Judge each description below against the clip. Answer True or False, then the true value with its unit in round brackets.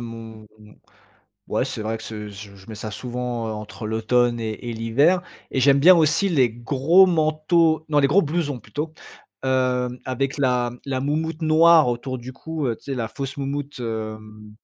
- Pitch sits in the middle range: False (130 Hz)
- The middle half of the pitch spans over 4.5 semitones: True (5.2 semitones)